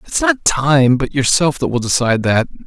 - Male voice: Yes, male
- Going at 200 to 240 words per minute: Yes, fast, 205 wpm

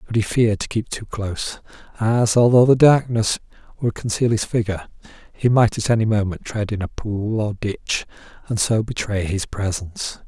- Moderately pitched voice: No, low, 110 Hz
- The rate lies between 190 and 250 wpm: No, average, 180 wpm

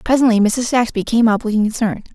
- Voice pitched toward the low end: No, high, 225 Hz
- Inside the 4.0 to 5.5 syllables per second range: No, 6.7 syllables/s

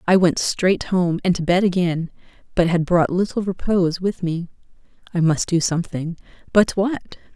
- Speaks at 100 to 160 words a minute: Yes, average, 155 wpm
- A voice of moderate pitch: Yes, medium, 180 Hz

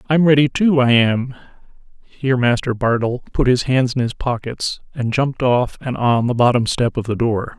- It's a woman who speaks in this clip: No, male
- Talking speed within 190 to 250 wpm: Yes, average, 200 wpm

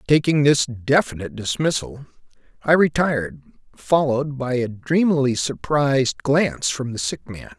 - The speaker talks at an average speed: No, slow, 125 wpm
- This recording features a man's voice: Yes, male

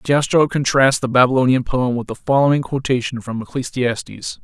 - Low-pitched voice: Yes, low, 130 Hz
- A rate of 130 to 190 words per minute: Yes, average, 150 wpm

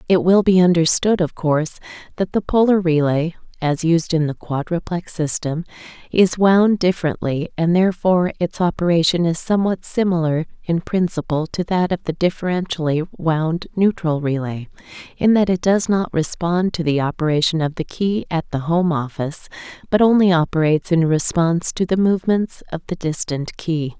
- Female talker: Yes, female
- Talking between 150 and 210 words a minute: Yes, average, 160 wpm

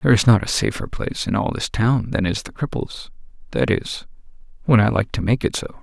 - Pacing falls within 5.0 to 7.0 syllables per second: Yes, 5.7 syllables/s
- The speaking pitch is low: Yes, low, 110 Hz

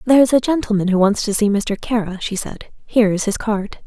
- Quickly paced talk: Yes, fast, 235 wpm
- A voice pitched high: Yes, high, 215 Hz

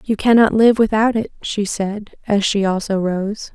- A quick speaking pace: No, average, 185 wpm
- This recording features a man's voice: No, female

